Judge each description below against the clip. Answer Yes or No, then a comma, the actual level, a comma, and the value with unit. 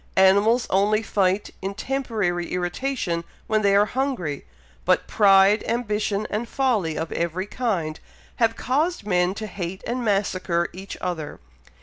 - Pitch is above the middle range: Yes, high, 200 Hz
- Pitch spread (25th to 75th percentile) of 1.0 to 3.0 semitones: No, average, 3.9 semitones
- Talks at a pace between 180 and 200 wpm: No, slow, 135 wpm